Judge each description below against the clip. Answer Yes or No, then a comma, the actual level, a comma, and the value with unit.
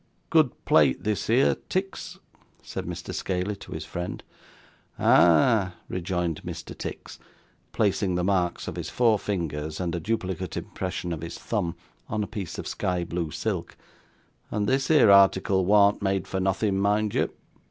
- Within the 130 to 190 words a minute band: Yes, average, 155 wpm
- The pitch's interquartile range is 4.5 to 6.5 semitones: No, average, 3.2 semitones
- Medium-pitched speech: No, very low, 95 Hz